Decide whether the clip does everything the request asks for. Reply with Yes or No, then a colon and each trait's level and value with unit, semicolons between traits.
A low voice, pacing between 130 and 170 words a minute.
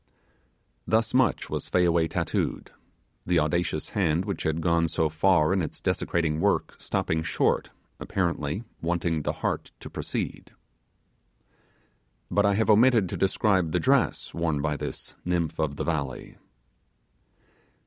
Yes: very low, 85 Hz; slow, 135 wpm